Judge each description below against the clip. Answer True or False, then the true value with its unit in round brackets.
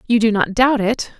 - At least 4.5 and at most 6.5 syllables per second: True (5.2 syllables/s)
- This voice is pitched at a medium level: False (225 Hz)